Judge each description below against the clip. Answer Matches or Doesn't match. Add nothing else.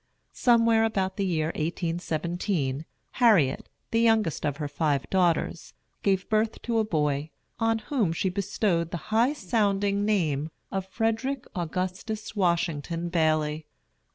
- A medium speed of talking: Doesn't match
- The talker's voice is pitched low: Doesn't match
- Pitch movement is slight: Doesn't match